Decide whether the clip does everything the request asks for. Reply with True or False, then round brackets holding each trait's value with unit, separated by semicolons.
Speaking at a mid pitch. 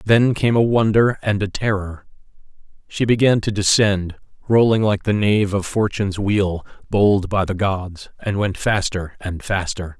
False (100 Hz)